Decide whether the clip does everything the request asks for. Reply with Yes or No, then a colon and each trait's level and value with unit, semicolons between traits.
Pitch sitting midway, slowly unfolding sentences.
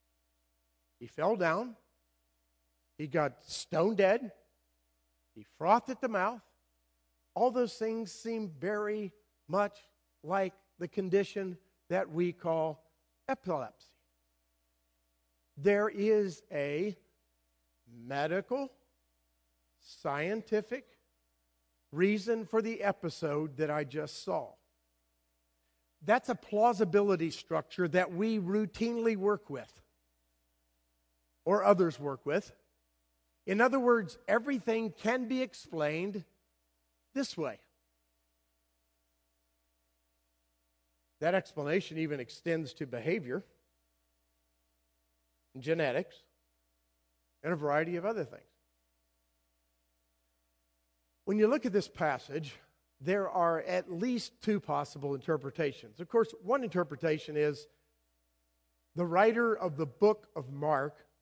Yes: medium, 145 Hz; slow, 95 wpm